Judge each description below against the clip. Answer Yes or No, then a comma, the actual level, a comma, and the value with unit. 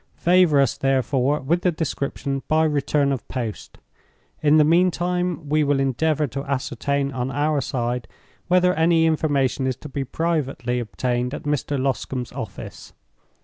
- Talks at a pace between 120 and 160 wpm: Yes, average, 145 wpm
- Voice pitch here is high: No, medium, 140 Hz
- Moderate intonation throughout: Yes, average, 3.2 semitones